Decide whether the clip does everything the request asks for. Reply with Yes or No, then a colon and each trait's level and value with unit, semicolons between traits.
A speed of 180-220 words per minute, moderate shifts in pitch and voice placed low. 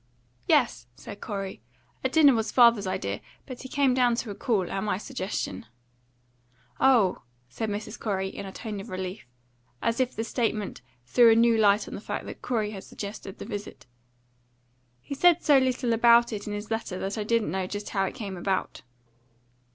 No: average, 190 wpm; average, 3.5 semitones; high, 215 Hz